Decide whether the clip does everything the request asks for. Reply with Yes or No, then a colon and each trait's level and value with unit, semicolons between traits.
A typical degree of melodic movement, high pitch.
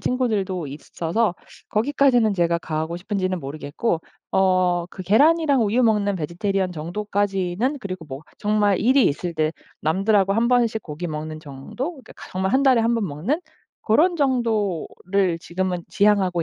Yes: average, 4.9 semitones; high, 195 Hz